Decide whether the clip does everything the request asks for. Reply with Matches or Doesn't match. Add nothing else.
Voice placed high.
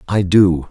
Doesn't match